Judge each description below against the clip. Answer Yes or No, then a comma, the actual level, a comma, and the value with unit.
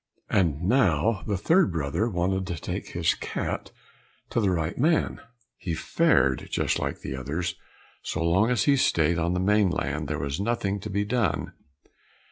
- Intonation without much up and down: No, average, 4.6 semitones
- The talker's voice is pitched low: Yes, very low, 90 Hz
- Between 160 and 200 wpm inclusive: Yes, average, 165 wpm